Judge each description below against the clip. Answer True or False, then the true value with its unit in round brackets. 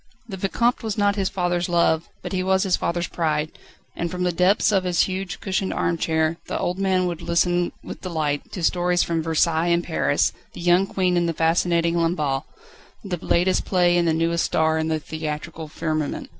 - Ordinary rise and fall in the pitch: False (2.2 semitones)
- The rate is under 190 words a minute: False (200 wpm)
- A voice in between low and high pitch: True (175 Hz)